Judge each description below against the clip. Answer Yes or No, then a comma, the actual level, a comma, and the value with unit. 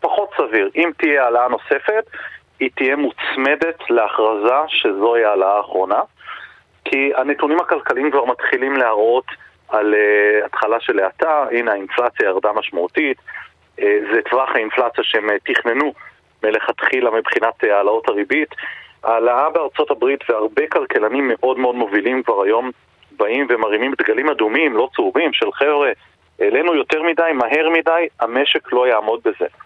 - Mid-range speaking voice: Yes, medium, 165 Hz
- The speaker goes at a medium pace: Yes, average, 125 wpm